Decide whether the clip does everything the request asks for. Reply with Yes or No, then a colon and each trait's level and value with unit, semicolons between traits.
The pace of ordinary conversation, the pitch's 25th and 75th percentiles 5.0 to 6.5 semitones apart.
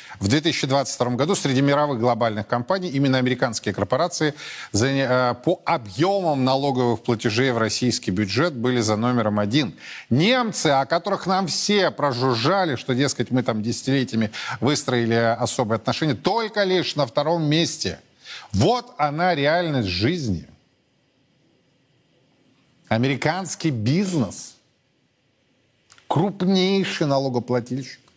No: slow, 100 wpm; average, 5.3 semitones